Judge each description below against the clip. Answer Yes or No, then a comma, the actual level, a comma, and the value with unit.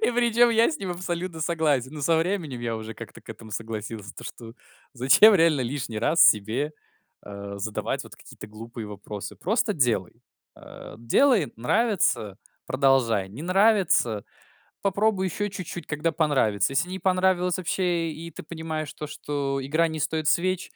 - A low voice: No, medium, 155 Hz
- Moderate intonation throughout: No, wide, 7.9 semitones